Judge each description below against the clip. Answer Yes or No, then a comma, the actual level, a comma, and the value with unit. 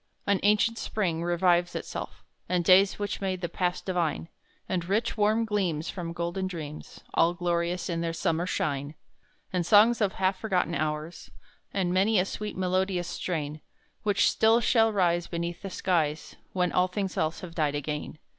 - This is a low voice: No, medium, 180 Hz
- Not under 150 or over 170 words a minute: Yes, average, 165 wpm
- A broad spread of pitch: No, average, 2.7 semitones